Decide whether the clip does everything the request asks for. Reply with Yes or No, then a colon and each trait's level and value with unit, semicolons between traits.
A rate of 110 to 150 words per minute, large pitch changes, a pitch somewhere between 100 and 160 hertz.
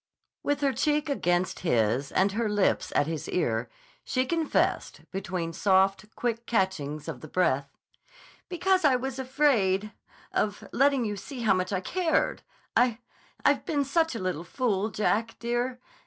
No: average, 145 wpm; wide, 6.3 semitones; high, 215 Hz